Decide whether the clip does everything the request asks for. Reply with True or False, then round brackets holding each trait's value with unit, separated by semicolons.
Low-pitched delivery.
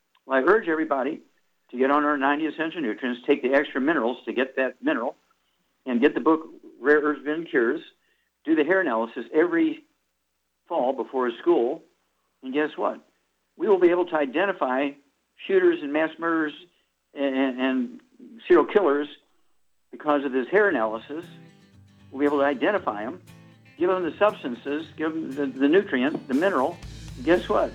False (150 Hz)